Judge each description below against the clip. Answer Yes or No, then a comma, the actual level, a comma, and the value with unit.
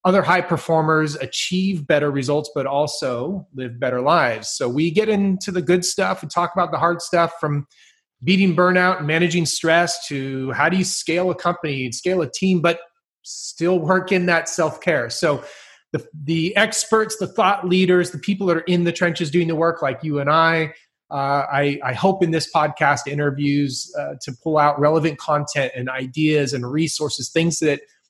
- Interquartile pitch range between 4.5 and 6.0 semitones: No, average, 3.6 semitones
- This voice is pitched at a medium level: Yes, medium, 165 Hz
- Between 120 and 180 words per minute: No, average, 190 wpm